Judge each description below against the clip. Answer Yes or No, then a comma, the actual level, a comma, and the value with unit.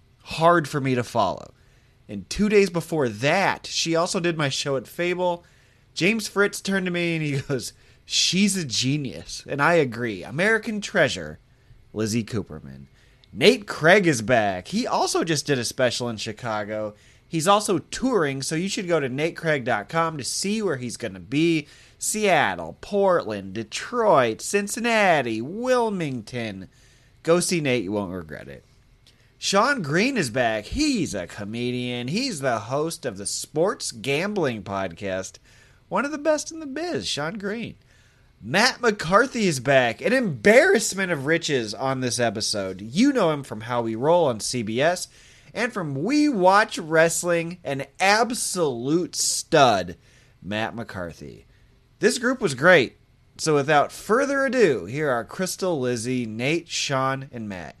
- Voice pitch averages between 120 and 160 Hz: Yes, medium, 140 Hz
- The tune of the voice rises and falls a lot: Yes, wide, 8.2 semitones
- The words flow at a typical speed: Yes, average, 150 wpm